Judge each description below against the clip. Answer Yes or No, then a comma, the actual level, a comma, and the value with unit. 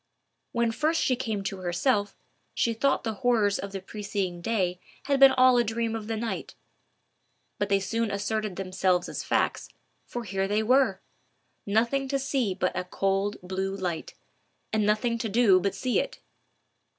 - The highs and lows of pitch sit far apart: No, average, 3.5 semitones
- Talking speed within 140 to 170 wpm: Yes, average, 165 wpm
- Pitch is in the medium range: No, high, 215 Hz